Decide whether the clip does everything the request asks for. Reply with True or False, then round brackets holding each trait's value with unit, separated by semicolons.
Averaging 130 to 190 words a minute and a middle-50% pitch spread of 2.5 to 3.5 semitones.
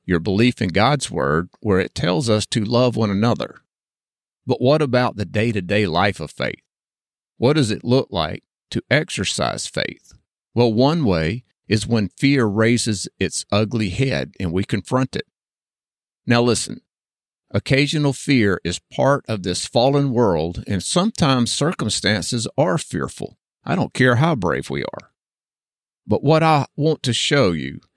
False (155 wpm; 4.9 semitones)